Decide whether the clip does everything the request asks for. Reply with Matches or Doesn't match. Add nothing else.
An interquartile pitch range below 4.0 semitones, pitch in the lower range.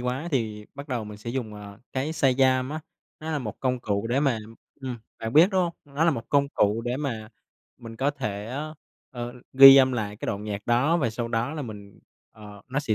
Doesn't match